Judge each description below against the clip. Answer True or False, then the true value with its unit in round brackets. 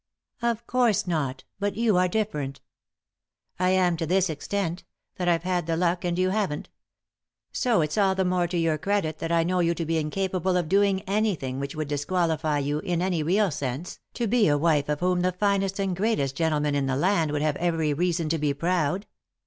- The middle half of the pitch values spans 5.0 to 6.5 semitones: False (3.8 semitones)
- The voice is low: False (175 Hz)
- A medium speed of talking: False (210 wpm)